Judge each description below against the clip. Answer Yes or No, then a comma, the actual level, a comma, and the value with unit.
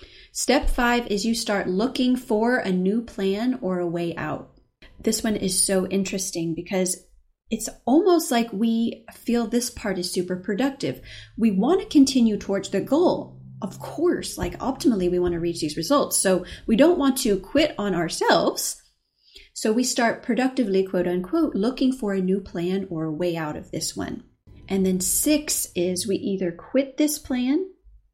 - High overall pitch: Yes, high, 210 Hz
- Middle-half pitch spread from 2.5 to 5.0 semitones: No, wide, 5.6 semitones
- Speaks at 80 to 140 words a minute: No, average, 175 wpm